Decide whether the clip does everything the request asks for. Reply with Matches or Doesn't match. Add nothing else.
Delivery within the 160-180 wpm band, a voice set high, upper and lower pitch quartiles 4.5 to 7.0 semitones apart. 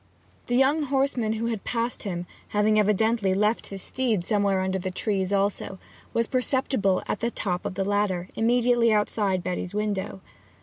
Doesn't match